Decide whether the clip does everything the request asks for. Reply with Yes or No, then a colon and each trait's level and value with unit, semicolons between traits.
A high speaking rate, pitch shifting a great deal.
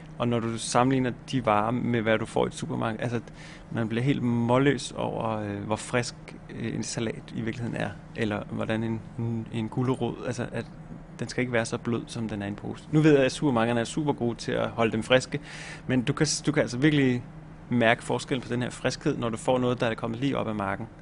No: fast, 235 wpm; average, 3.9 semitones